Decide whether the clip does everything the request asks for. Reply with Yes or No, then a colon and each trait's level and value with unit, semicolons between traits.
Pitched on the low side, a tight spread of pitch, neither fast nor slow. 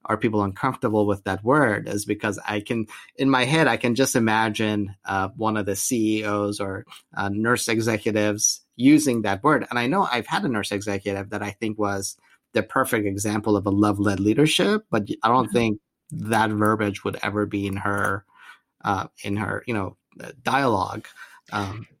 Yes: low, 105 Hz; narrow, 2.1 semitones; average, 180 wpm